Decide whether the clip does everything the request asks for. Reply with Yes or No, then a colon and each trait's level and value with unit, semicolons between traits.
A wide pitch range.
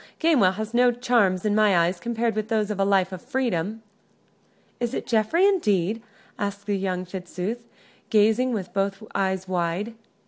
No: average, 3.7 semitones